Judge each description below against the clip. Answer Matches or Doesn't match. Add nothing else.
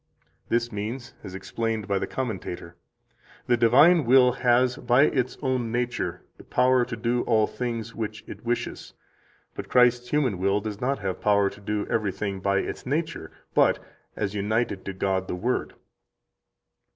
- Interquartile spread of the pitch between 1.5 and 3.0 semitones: Doesn't match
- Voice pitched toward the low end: Matches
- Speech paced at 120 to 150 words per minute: Doesn't match